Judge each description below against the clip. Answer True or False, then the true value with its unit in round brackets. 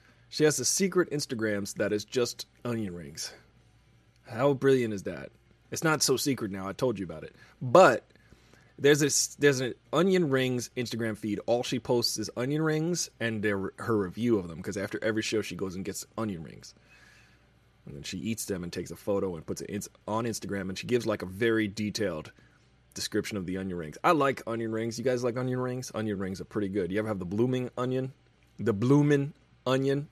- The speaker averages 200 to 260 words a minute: True (205 wpm)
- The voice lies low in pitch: True (115 Hz)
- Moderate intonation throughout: True (4.3 semitones)